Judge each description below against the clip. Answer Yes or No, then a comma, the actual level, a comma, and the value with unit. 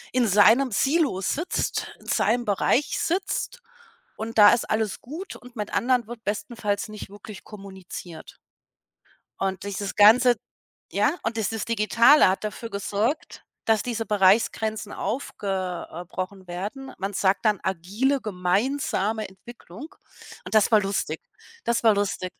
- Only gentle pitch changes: No, average, 3.5 semitones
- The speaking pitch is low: No, high, 215 Hz